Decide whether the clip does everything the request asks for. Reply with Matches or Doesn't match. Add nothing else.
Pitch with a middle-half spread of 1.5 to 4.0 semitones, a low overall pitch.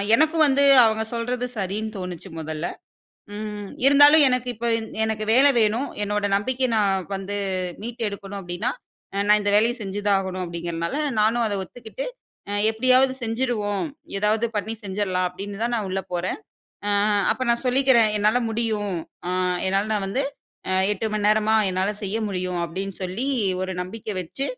Doesn't match